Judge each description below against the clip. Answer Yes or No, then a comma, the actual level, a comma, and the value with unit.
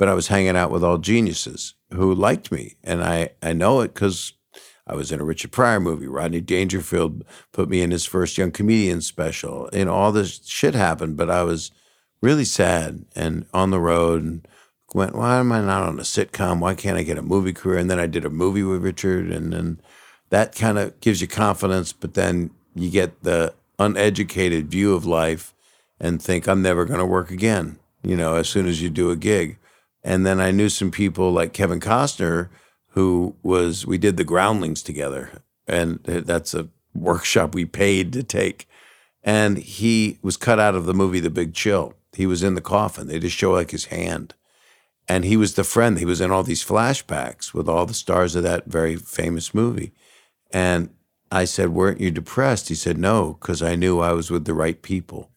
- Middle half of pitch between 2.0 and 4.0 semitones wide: Yes, narrow, 2.6 semitones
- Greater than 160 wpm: Yes, fast, 205 wpm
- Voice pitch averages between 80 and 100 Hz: Yes, very low, 90 Hz